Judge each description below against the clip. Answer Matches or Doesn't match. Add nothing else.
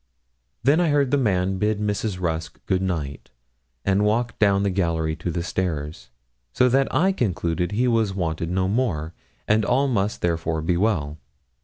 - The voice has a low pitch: Matches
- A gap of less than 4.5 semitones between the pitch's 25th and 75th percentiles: Doesn't match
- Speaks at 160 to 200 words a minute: Matches